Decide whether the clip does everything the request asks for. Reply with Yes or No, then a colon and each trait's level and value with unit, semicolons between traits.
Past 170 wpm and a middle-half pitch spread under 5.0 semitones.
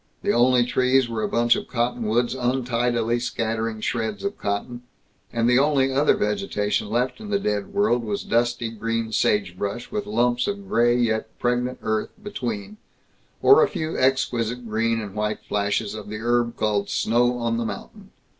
No: average, 165 wpm; narrow, 2.5 semitones